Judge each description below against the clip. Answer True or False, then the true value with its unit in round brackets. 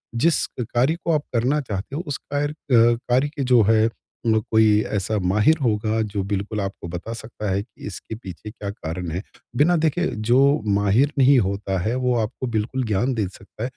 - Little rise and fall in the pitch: False (4.2 semitones)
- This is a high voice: False (110 Hz)